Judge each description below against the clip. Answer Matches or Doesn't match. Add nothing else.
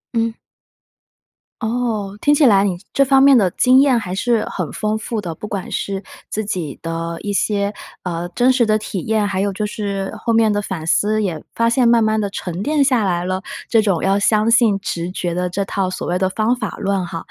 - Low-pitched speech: Doesn't match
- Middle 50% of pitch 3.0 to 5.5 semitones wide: Matches